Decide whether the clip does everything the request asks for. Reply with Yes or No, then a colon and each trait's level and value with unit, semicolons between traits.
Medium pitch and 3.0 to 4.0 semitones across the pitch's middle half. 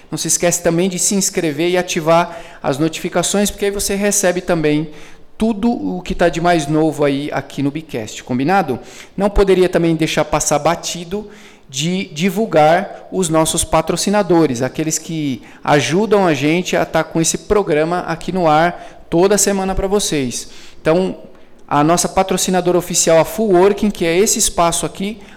Yes: medium, 175 Hz; average, 3.7 semitones